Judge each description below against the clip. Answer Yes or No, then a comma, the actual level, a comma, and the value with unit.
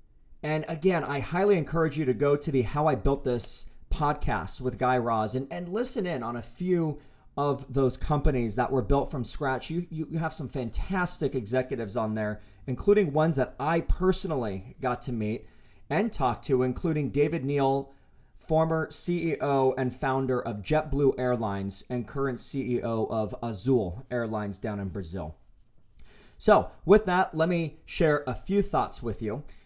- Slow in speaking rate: No, average, 165 wpm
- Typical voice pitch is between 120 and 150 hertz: Yes, low, 135 Hz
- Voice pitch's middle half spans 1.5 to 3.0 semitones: No, average, 4.7 semitones